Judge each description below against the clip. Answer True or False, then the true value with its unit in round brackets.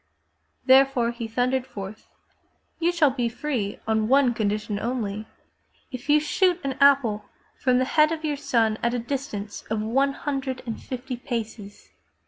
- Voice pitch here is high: True (250 Hz)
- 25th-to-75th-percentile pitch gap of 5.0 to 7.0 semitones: False (3.9 semitones)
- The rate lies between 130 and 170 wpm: True (160 wpm)